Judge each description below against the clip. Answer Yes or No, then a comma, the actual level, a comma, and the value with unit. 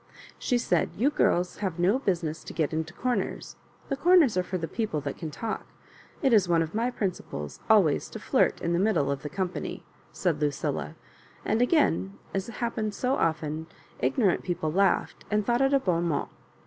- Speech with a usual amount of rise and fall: No, wide, 6.3 semitones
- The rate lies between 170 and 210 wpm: Yes, average, 190 wpm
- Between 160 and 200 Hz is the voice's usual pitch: Yes, medium, 185 Hz